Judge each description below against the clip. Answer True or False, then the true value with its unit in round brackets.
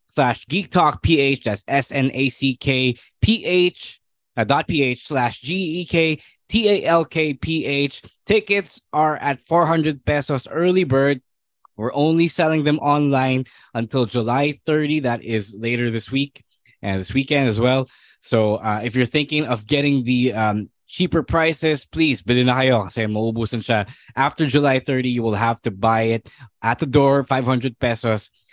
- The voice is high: False (135 Hz)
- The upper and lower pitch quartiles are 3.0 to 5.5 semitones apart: True (4.4 semitones)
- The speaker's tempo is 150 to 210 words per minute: False (135 wpm)